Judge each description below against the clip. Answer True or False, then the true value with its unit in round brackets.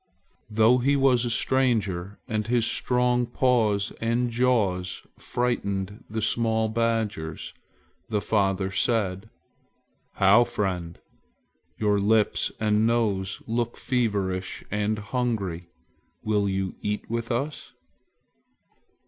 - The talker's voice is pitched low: True (110 Hz)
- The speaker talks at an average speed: False (105 wpm)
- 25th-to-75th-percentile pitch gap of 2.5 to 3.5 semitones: True (3.2 semitones)